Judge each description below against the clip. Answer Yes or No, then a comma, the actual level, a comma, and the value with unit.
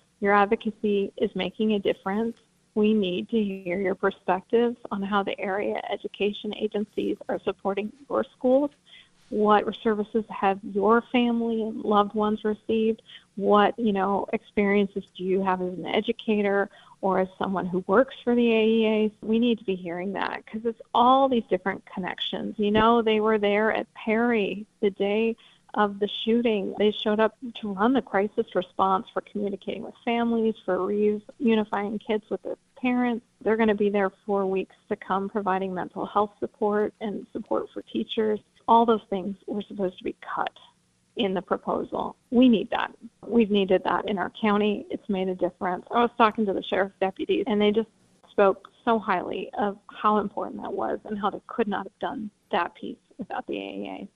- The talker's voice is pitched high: Yes, high, 210 Hz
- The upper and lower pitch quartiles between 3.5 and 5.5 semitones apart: No, narrow, 2.5 semitones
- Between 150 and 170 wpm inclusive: No, average, 180 wpm